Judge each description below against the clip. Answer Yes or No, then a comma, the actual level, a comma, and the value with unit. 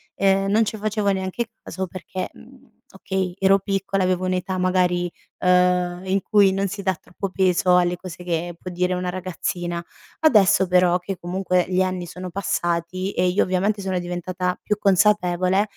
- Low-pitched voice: No, medium, 185 Hz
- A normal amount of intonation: No, narrow, 1.5 semitones